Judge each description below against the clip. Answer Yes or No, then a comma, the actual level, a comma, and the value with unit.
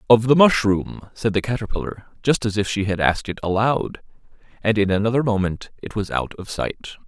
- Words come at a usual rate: Yes, average, 195 wpm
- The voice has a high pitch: No, low, 105 Hz